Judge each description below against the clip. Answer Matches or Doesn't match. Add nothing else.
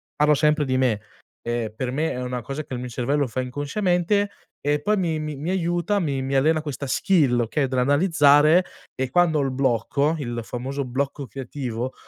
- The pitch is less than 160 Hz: Matches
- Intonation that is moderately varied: Matches